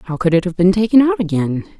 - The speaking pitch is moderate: Yes, medium, 180 Hz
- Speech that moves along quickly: Yes, fast, 270 wpm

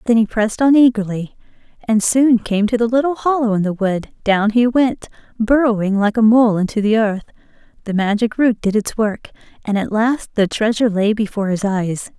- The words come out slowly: No, average, 195 wpm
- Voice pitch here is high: Yes, high, 220 Hz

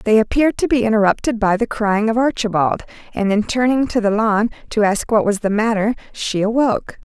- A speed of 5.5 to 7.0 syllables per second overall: Yes, 5.6 syllables/s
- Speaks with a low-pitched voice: No, high, 220 Hz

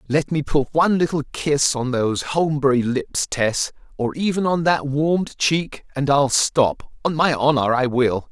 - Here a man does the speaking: Yes, male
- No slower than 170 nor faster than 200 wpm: Yes, average, 175 wpm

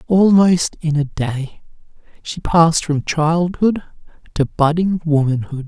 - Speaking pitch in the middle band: Yes, medium, 160 Hz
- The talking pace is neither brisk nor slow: No, slow, 115 wpm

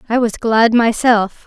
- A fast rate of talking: No, average, 165 wpm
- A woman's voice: Yes, female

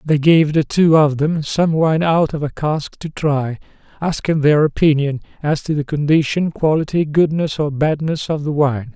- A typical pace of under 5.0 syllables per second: Yes, 4.5 syllables/s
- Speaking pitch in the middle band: Yes, medium, 150 Hz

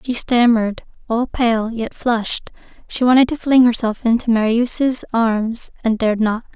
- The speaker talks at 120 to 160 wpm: Yes, average, 155 wpm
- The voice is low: No, high, 230 Hz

